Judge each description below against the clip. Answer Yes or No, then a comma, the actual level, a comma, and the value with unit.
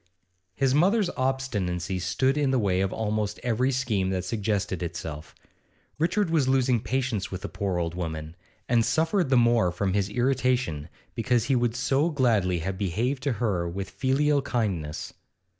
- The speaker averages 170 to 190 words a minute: No, average, 160 wpm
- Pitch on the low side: Yes, low, 115 Hz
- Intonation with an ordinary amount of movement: No, wide, 6.1 semitones